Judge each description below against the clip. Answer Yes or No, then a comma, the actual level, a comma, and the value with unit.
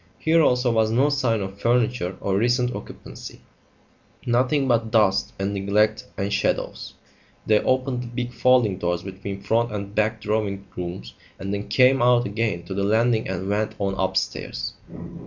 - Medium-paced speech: Yes, average, 160 wpm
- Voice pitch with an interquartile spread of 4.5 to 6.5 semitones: No, average, 3.8 semitones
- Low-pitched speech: Yes, low, 110 Hz